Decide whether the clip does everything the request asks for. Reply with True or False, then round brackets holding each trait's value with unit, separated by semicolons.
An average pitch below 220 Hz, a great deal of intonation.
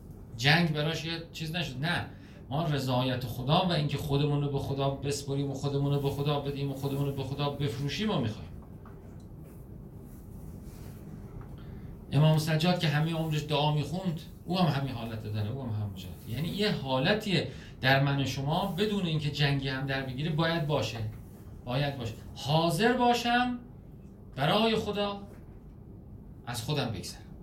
False (140 Hz; 4.1 semitones)